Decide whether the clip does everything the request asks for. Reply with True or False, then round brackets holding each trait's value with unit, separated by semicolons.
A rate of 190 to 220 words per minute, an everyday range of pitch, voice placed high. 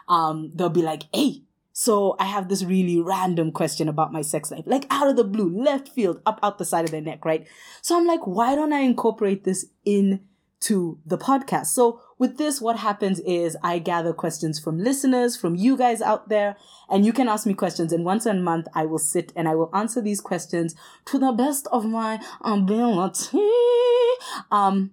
False (200 wpm; 5.9 semitones; 200 Hz)